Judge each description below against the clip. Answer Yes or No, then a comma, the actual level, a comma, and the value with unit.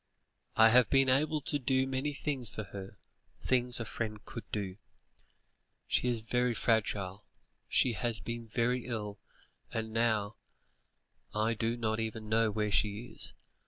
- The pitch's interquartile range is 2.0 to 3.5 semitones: Yes, narrow, 2.5 semitones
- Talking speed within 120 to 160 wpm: Yes, average, 150 wpm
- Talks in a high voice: No, low, 115 Hz